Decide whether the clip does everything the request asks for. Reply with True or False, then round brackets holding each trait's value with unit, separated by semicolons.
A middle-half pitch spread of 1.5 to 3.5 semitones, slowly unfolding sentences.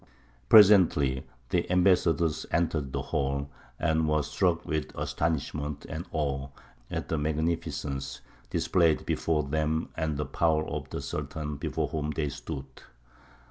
True (2.4 semitones; 130 wpm)